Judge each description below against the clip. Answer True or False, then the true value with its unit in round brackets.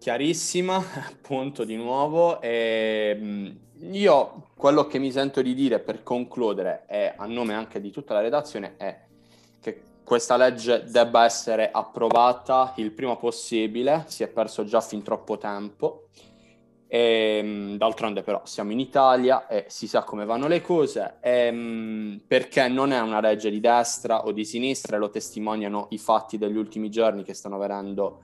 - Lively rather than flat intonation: False (3.2 semitones)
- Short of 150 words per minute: False (155 wpm)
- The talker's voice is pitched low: True (115 Hz)